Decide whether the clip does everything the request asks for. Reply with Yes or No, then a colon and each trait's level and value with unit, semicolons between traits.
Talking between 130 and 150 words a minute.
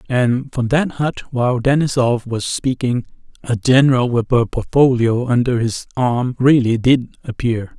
Yes: average, 145 wpm